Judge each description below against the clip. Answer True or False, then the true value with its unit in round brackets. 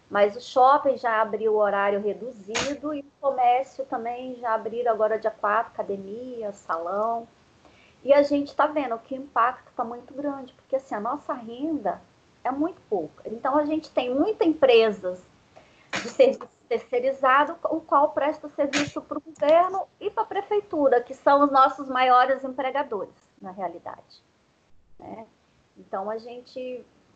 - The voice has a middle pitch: False (265 Hz)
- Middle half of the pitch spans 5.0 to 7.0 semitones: False (4.2 semitones)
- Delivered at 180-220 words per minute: False (155 wpm)